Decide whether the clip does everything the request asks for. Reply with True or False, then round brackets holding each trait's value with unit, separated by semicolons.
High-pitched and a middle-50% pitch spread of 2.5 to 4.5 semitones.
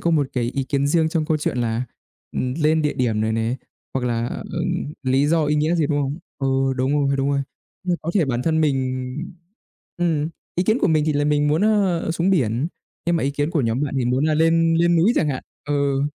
False (145 Hz; 3.6 semitones)